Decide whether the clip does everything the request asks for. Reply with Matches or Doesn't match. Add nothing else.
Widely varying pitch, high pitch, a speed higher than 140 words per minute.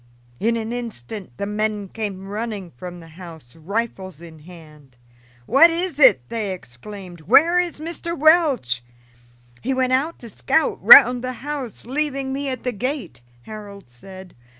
Matches